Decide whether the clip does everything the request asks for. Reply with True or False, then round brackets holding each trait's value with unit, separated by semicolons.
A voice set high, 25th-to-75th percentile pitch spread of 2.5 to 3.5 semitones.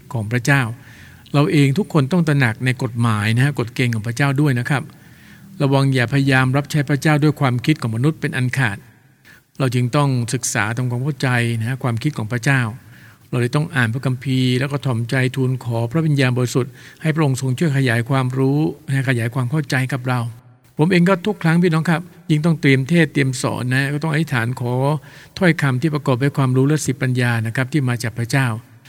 False (135 Hz; 2.9 semitones)